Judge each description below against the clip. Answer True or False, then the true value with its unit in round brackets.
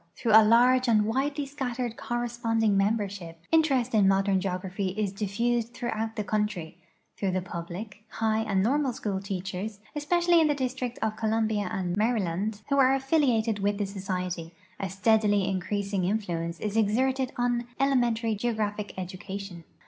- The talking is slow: False (155 wpm)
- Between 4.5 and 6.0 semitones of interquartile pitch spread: False (3.7 semitones)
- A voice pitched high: True (215 Hz)